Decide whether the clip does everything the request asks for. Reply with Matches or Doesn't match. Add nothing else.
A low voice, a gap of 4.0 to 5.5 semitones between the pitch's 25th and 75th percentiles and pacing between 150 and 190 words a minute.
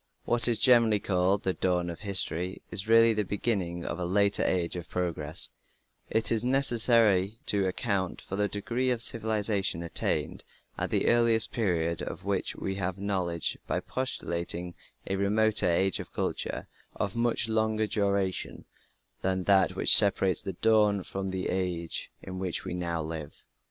Doesn't match